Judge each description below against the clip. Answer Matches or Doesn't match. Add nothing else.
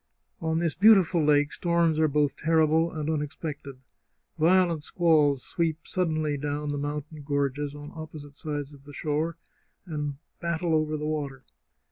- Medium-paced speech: Matches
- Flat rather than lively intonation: Matches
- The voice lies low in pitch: Doesn't match